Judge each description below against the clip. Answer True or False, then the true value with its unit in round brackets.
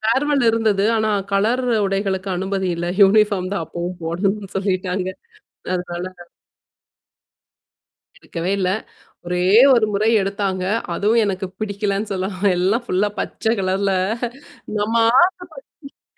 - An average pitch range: False (2.3 semitones)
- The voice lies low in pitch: False (195 Hz)